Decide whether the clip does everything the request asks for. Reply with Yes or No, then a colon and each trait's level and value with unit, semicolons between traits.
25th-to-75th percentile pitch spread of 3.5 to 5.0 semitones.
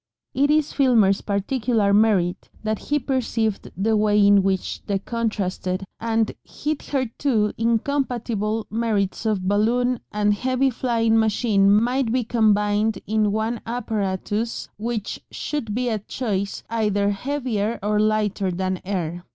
No: average, 2.7 semitones